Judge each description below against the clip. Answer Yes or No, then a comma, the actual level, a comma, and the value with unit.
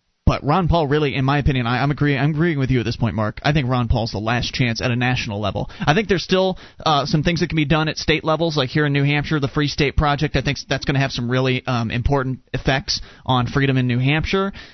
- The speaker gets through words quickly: Yes, fast, 275 wpm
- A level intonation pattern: No, average, 3.3 semitones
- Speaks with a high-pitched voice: No, medium, 140 Hz